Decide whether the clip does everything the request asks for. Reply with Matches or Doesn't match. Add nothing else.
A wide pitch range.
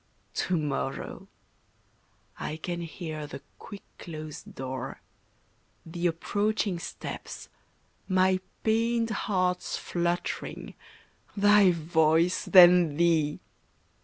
Doesn't match